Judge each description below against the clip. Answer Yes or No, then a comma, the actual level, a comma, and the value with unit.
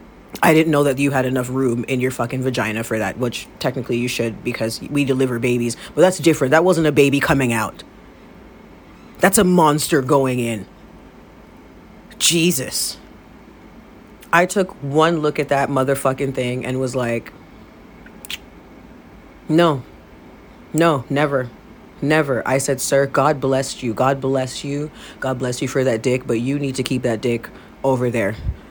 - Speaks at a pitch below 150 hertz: Yes, low, 135 Hz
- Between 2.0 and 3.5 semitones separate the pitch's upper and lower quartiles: Yes, average, 2.8 semitones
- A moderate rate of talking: Yes, average, 160 wpm